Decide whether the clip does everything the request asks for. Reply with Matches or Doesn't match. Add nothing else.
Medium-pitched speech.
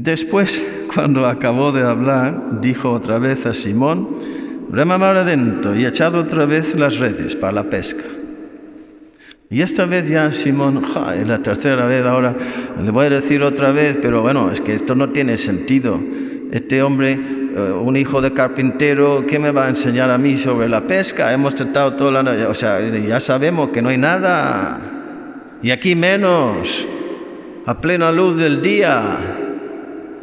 Matches